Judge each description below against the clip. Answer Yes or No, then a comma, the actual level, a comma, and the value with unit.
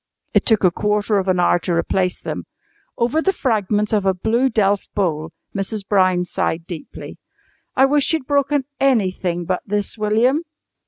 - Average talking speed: Yes, average, 165 wpm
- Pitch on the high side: Yes, high, 205 Hz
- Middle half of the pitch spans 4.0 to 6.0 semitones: Yes, average, 4.8 semitones